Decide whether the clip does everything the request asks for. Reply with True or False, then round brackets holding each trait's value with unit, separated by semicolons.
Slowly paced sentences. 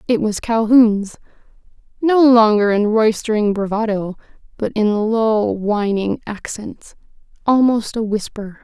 True (105 wpm)